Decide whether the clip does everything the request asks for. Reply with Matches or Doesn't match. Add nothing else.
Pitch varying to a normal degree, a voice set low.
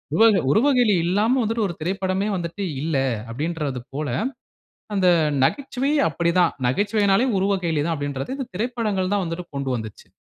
Doesn't match